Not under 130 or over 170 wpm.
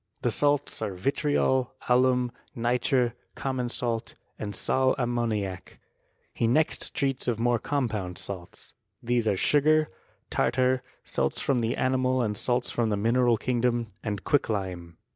Yes: slow, 135 wpm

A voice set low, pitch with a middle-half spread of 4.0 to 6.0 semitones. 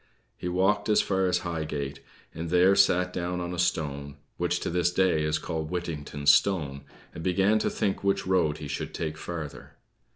No: very low, 85 Hz; average, 3.1 semitones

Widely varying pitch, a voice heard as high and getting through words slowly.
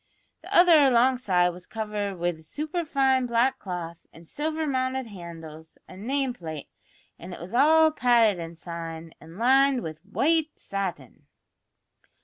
Yes: wide, 7.9 semitones; high, 215 Hz; slow, 130 wpm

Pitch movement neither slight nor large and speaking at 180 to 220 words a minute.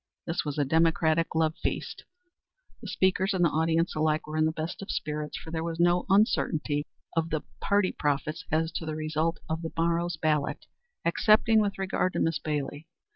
No: narrow, 1.9 semitones; average, 200 wpm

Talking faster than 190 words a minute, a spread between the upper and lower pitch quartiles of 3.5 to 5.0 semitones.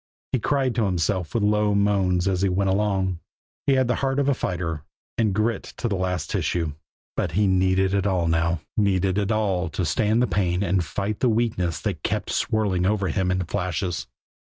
No: average, 200 wpm; average, 2.8 semitones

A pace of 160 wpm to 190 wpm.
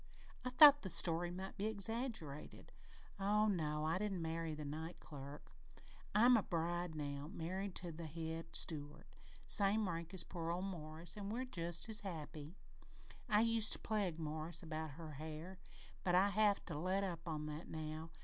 Yes: average, 170 wpm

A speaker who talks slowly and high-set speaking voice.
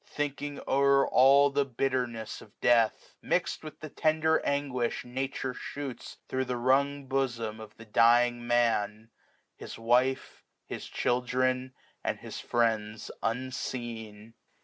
No: slow, 125 wpm; low, 125 Hz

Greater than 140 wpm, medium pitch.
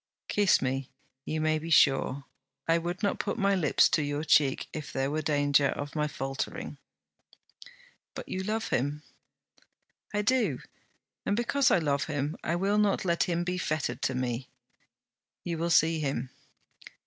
Yes: average, 160 wpm; medium, 155 Hz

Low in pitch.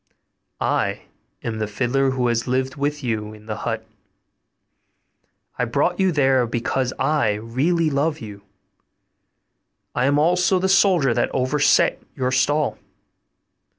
Yes: low, 130 Hz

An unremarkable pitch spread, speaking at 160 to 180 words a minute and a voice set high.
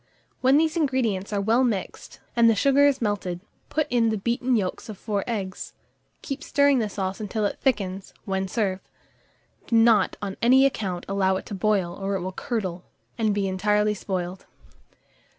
Yes: average, 3.8 semitones; average, 175 wpm; high, 210 Hz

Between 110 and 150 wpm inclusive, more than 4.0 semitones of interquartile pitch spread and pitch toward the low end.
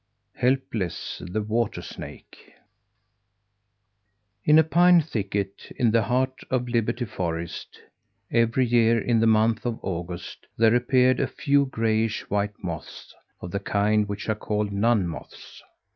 No: slow, 135 wpm; average, 3.3 semitones; low, 110 Hz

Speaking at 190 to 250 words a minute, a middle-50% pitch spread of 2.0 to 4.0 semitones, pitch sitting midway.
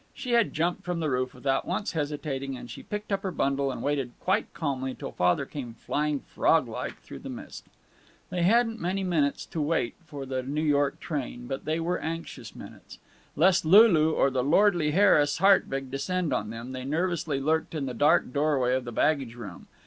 No: average, 195 wpm; average, 4.5 semitones; medium, 150 Hz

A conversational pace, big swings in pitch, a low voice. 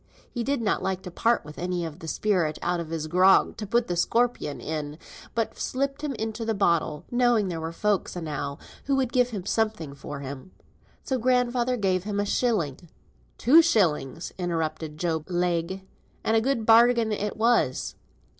No: average, 180 wpm; wide, 6.3 semitones; high, 195 Hz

